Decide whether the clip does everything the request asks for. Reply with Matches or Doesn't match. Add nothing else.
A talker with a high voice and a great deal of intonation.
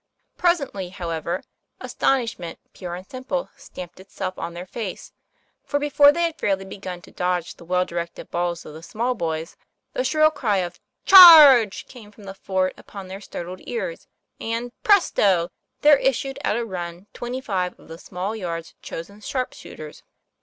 Matches